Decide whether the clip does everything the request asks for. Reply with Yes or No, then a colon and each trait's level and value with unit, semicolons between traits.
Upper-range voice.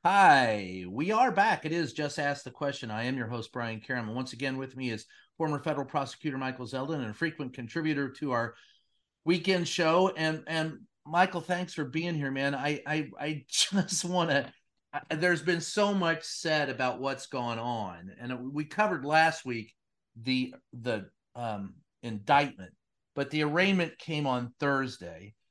No: medium, 140 Hz